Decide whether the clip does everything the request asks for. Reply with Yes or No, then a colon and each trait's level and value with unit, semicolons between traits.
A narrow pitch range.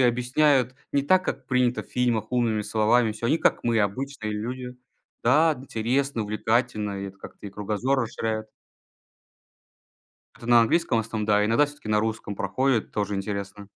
No: average, 3.2 semitones